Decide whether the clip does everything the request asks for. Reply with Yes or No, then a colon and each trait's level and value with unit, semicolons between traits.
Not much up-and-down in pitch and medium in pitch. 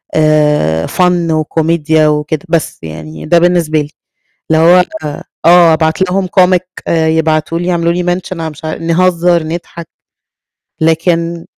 Yes: narrow, 1.8 semitones; medium, 165 Hz